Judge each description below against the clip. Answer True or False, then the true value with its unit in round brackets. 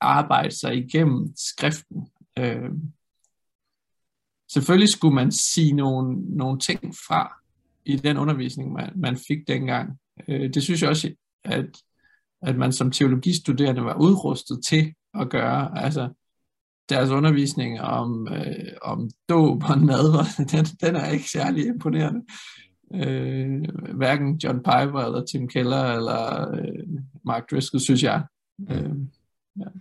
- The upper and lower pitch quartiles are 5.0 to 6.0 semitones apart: False (3.9 semitones)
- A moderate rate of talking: False (135 wpm)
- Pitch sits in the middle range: True (145 Hz)